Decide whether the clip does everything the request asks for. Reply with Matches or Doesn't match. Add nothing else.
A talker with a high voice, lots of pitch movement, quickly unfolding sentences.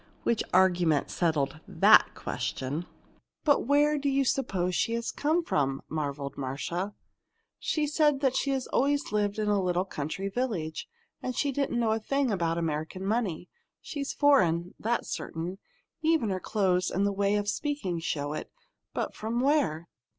Doesn't match